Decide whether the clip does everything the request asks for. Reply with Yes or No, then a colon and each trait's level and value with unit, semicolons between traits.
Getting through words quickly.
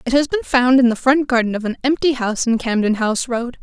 Yes: fast, 265 wpm